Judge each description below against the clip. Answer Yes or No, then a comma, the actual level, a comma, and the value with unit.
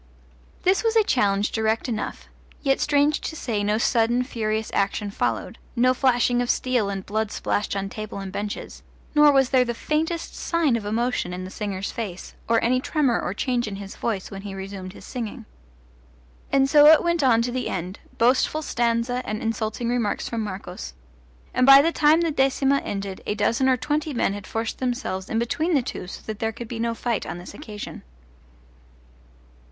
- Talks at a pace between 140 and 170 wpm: No, average, 190 wpm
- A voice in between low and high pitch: No, high, 230 Hz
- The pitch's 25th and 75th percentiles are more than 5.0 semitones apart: No, average, 4.5 semitones